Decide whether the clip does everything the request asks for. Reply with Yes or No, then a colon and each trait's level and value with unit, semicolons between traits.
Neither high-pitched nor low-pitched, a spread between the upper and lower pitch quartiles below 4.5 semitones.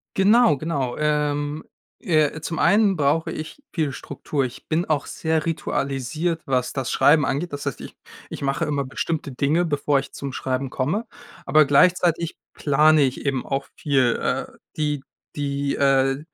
Yes: medium, 145 Hz; narrow, 2.6 semitones